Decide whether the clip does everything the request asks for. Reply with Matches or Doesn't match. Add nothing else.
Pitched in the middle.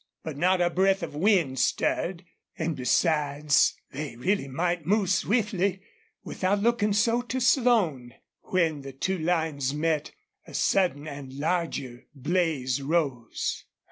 Matches